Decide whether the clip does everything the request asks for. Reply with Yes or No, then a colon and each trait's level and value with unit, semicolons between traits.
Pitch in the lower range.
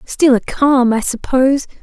No: very high, 260 Hz